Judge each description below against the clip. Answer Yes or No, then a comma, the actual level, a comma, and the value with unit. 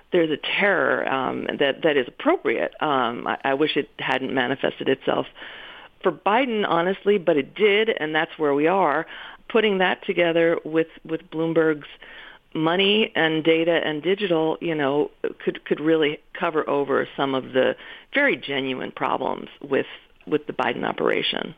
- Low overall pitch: No, medium, 160 Hz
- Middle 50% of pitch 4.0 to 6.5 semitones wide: Yes, average, 4.6 semitones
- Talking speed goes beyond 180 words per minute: No, average, 155 wpm